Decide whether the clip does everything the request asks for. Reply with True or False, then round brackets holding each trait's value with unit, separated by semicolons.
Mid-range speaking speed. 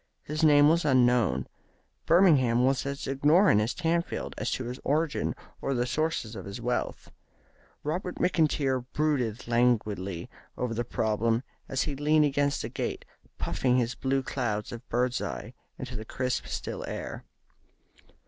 True (150 wpm)